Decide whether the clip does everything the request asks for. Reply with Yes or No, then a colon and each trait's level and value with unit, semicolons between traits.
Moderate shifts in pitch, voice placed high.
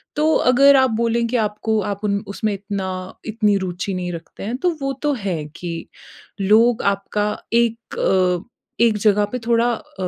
Yes: average, 3.4 semitones; high, 210 Hz